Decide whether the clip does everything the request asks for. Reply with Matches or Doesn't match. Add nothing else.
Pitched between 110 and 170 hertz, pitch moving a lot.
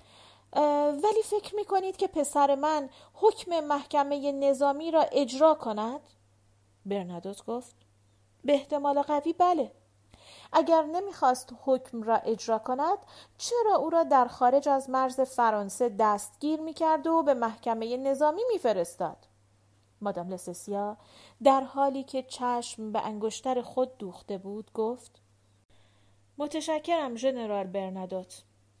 Doesn't match